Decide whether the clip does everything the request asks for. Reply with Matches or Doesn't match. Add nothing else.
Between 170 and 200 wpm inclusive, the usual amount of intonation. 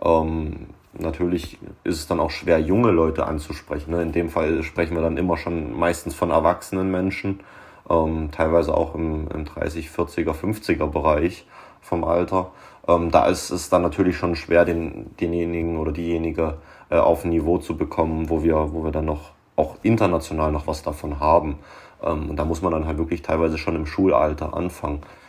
Doesn't match